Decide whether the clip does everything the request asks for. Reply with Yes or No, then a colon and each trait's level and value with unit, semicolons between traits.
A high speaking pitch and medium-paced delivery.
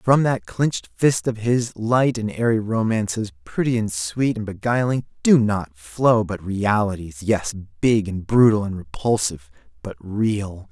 No: low, 110 Hz; average, 150 wpm